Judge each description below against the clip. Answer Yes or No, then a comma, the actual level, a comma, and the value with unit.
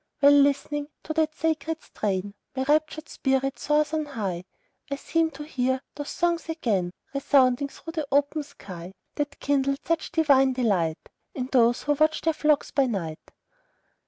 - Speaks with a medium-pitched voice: No, very high, 280 Hz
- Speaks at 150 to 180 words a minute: Yes, average, 160 wpm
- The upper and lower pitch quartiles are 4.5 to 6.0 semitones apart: No, average, 3.4 semitones